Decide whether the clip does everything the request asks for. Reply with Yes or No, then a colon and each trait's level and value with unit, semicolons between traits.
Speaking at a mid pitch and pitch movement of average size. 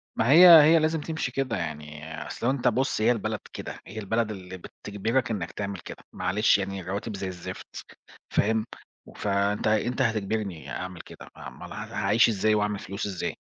No: low, 105 Hz; average, 3.2 semitones